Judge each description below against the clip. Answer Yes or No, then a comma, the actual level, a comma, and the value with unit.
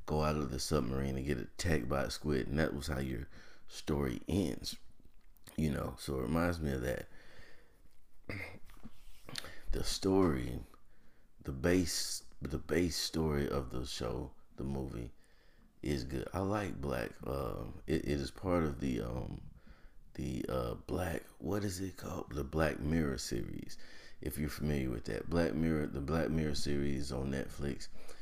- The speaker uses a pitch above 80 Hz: No, very low, 75 Hz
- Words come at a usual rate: Yes, average, 160 wpm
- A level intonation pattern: No, average, 3.3 semitones